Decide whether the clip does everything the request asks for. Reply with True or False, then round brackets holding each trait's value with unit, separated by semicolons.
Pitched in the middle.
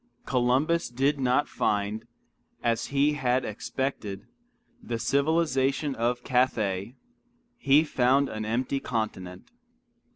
False (125 Hz)